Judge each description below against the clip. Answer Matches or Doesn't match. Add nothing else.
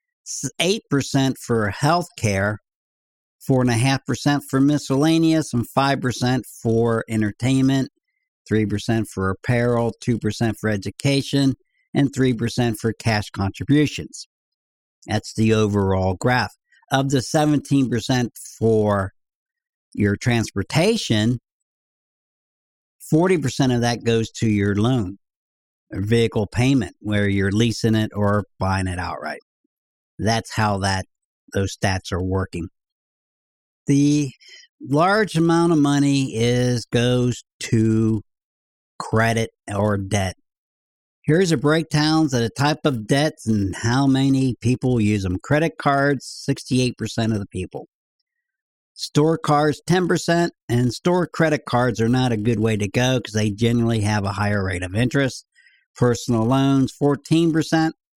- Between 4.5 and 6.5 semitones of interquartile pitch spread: Matches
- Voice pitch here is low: Matches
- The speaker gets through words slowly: Matches